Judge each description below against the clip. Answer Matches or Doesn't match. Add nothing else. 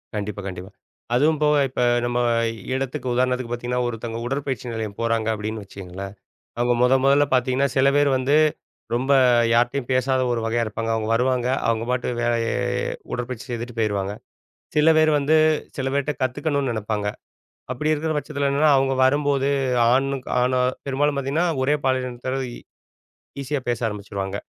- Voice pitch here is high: Doesn't match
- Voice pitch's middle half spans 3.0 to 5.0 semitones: Matches